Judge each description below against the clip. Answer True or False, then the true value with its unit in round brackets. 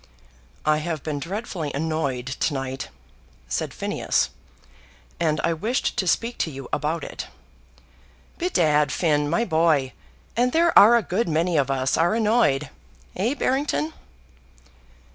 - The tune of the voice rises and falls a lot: True (6.3 semitones)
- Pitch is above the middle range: False (160 Hz)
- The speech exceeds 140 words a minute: False (135 wpm)